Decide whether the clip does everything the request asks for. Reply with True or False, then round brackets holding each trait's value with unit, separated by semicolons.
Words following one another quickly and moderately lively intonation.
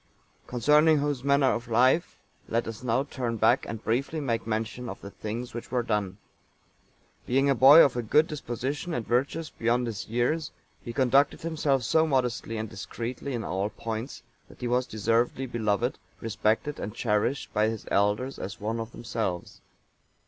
False (170 wpm; 3.4 semitones)